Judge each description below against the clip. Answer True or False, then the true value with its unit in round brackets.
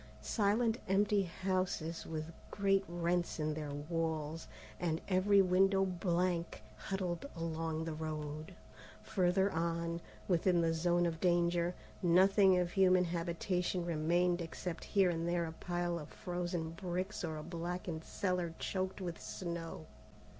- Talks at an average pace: False (130 wpm)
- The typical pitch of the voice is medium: True (175 Hz)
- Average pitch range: False (2.0 semitones)